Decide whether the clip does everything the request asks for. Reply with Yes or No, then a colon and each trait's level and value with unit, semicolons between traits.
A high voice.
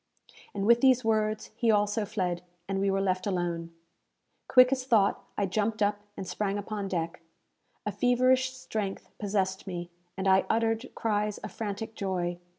Yes: high, 205 Hz